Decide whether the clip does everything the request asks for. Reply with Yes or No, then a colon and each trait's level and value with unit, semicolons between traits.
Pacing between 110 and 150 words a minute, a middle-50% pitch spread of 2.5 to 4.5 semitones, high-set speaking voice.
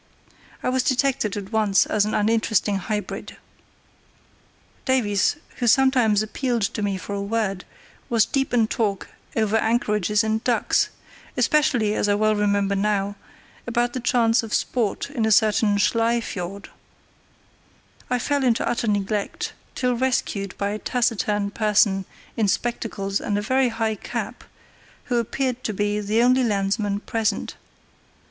Yes: average, 145 wpm; average, 2.8 semitones; high, 215 Hz